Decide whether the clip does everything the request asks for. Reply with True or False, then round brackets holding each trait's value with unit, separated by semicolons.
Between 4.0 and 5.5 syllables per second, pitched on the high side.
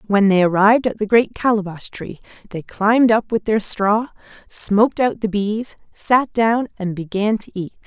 True (4.7 syllables/s; 210 Hz)